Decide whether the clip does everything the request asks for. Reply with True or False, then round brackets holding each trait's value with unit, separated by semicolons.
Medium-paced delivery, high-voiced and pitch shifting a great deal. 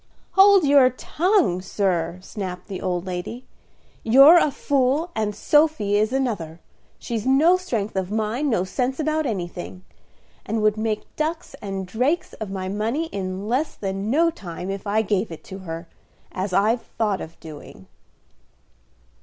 True (155 wpm; 215 Hz; 6.4 semitones)